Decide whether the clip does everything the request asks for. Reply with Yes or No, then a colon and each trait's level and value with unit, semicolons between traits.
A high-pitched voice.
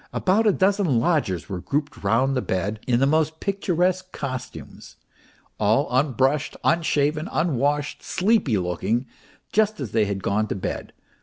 No: medium, 140 Hz